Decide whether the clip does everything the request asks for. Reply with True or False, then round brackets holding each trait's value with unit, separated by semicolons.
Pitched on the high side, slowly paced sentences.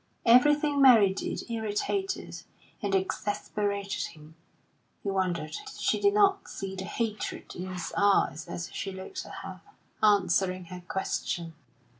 True (200 Hz; 130 wpm)